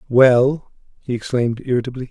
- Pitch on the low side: Yes, low, 125 Hz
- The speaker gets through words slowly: Yes, slow, 115 wpm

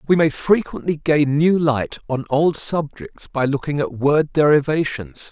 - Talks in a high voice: No, medium, 150 Hz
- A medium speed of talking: Yes, average, 160 wpm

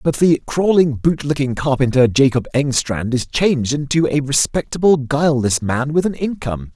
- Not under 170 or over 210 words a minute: No, average, 150 wpm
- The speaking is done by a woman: No, male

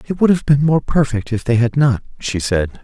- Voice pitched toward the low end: Yes, low, 130 Hz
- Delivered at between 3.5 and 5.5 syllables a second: Yes, 5.1 syllables/s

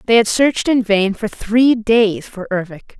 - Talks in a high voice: Yes, high, 215 Hz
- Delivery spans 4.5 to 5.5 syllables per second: No, 4.3 syllables/s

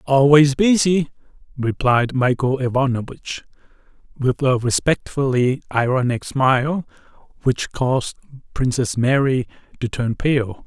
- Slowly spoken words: Yes, slow, 95 wpm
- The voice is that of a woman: No, male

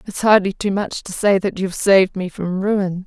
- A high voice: Yes, high, 195 Hz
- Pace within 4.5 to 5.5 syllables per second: Yes, 5.1 syllables/s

